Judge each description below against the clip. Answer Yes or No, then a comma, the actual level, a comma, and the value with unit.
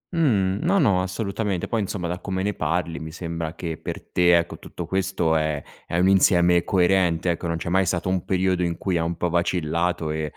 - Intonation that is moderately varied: No, narrow, 2.2 semitones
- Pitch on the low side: Yes, very low, 90 Hz